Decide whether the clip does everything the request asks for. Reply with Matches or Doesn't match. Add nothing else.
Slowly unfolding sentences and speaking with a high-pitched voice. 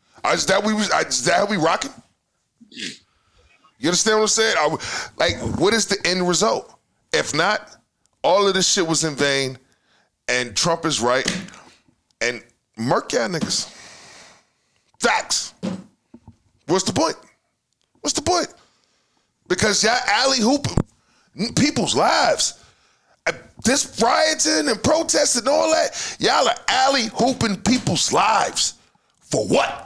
Matches